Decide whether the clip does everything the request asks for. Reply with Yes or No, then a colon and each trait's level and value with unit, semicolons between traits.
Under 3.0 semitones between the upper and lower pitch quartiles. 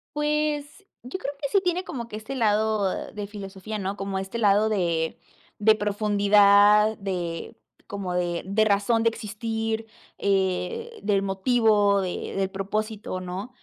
Yes: narrow, 2.5 semitones